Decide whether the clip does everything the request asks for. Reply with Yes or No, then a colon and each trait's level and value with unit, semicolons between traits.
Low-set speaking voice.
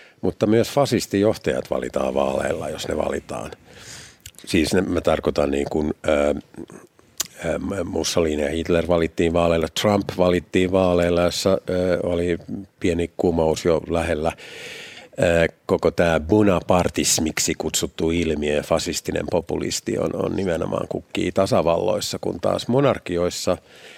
Yes: very low, 85 Hz